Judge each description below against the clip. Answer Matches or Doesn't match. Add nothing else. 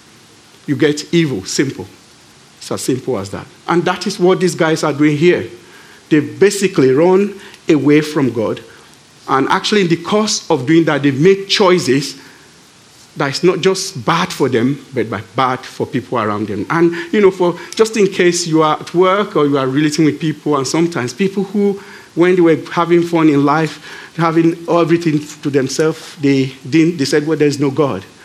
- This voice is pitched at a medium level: Matches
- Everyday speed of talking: Matches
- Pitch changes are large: Doesn't match